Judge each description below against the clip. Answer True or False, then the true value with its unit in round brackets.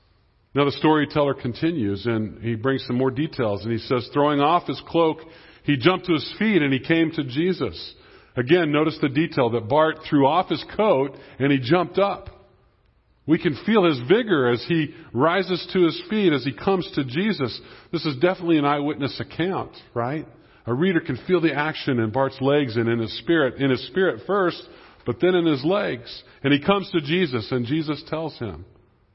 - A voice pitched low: False (145 Hz)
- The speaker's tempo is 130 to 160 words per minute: False (195 wpm)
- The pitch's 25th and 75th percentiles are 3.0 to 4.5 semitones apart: False (5.0 semitones)